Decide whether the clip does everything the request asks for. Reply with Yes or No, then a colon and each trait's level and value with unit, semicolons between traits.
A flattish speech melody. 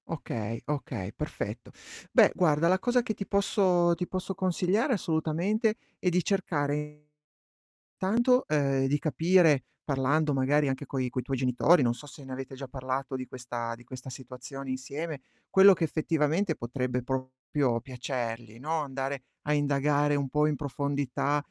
No: average, 4.2 semitones